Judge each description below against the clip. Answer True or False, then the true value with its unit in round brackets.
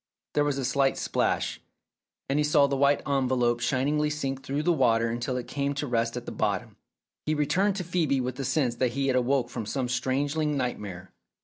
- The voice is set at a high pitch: False (135 Hz)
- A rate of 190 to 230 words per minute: True (205 wpm)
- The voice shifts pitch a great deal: False (2.9 semitones)